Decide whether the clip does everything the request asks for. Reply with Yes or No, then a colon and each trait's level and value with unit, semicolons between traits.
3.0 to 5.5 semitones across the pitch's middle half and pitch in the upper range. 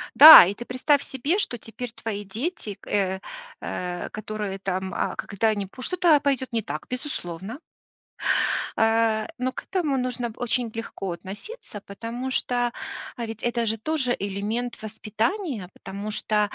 Yes: average, 3.8 semitones; high, 225 Hz